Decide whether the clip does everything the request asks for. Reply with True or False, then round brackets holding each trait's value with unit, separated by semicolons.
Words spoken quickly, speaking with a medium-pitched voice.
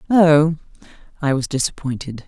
False (105 wpm; 145 Hz)